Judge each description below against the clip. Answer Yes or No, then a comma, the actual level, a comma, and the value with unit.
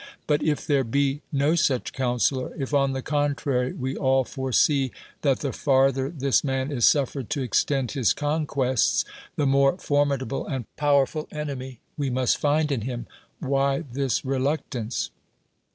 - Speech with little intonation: Yes, narrow, 1.7 semitones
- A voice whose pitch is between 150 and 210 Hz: No, low, 135 Hz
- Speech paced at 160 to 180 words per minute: No, average, 150 wpm